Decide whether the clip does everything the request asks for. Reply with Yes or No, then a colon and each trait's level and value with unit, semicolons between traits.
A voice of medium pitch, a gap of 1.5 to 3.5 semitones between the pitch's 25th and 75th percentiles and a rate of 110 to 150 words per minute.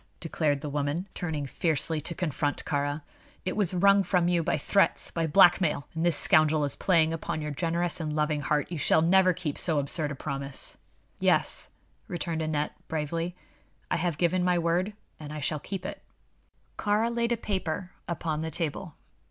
No: medium, 165 Hz; average, 2.9 semitones; average, 175 wpm